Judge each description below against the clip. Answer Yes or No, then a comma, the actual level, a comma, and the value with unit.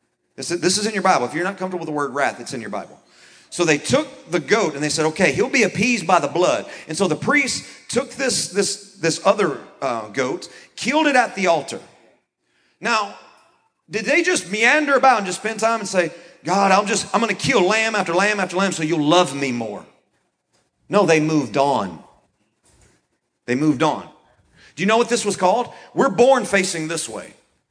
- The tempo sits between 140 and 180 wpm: No, fast, 205 wpm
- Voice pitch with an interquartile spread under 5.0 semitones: No, wide, 5.5 semitones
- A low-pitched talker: No, high, 190 Hz